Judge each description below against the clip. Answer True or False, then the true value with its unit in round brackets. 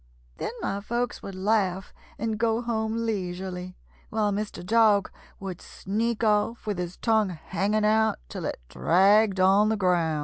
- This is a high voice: True (205 Hz)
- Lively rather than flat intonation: False (2.8 semitones)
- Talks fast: False (150 wpm)